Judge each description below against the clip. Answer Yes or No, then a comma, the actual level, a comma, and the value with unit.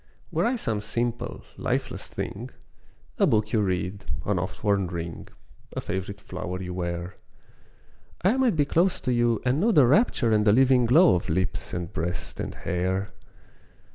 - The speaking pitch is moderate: No, low, 105 Hz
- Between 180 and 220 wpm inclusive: No, average, 170 wpm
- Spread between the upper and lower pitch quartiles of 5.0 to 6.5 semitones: Yes, wide, 5.4 semitones